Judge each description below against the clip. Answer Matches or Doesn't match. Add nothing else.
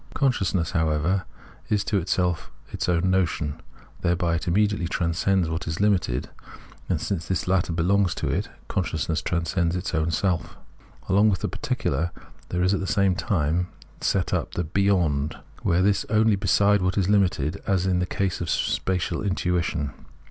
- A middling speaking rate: Matches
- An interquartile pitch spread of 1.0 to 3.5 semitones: Matches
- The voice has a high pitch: Doesn't match